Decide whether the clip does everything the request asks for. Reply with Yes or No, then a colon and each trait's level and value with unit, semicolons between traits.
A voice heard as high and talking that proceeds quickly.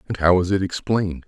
No: very low, 90 Hz; fast, 235 wpm